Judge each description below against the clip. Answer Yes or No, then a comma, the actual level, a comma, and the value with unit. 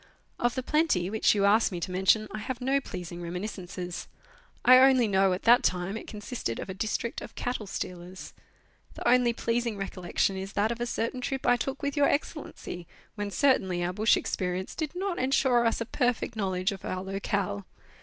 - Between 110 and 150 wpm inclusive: No, average, 195 wpm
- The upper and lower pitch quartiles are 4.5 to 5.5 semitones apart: Yes, average, 4.9 semitones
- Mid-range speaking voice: No, high, 215 Hz